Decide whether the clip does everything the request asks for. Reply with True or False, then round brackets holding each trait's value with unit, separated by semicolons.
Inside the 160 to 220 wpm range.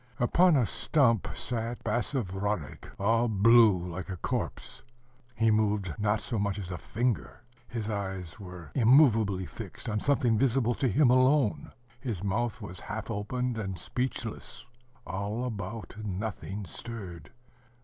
False (135 wpm)